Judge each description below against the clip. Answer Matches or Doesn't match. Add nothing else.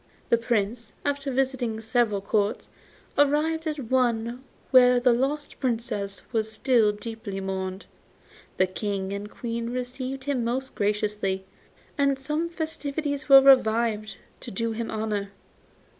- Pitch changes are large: Doesn't match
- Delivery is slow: Matches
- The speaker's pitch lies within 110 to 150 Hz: Doesn't match